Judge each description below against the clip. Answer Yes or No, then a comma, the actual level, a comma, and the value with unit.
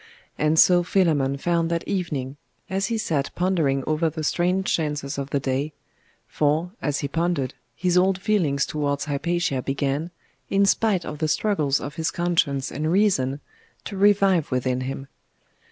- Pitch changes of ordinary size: Yes, average, 4.4 semitones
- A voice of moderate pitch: Yes, medium, 155 Hz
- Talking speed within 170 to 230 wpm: No, average, 155 wpm